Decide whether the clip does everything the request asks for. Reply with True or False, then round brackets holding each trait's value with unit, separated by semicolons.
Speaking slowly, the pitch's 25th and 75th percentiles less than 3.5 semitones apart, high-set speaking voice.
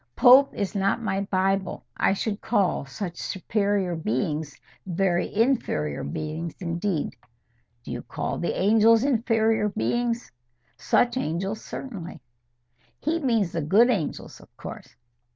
False (125 wpm; 4.9 semitones; 195 Hz)